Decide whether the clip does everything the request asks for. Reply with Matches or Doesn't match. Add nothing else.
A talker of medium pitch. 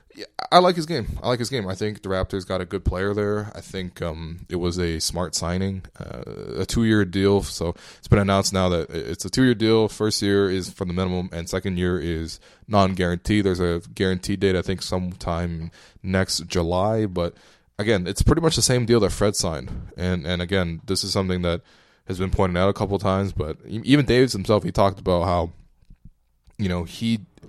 Doesn't match